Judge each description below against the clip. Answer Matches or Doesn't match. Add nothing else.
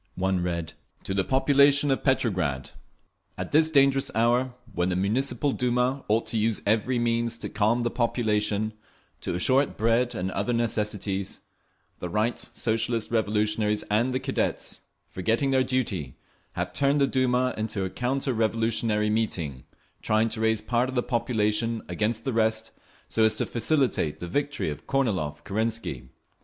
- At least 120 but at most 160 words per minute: Matches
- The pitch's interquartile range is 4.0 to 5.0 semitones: Doesn't match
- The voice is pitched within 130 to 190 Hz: Doesn't match